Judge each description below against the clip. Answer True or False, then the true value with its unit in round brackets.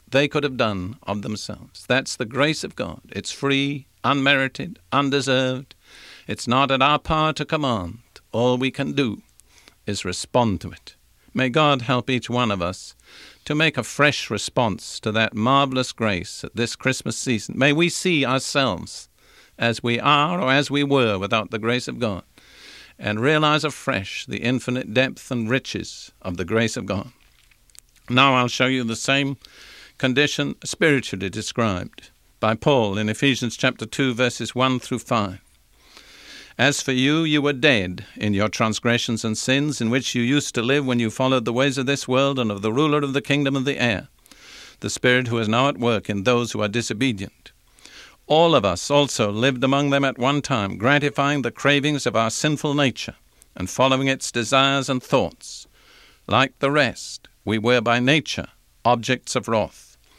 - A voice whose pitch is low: True (125 Hz)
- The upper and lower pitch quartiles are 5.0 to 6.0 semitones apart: False (3.9 semitones)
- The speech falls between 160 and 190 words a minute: True (175 wpm)